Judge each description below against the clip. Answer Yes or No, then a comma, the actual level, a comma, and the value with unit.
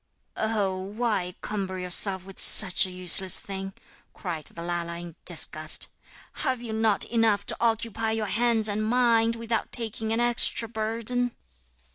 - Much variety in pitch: No, average, 3.3 semitones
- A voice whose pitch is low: No, high, 215 Hz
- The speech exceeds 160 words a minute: No, average, 145 wpm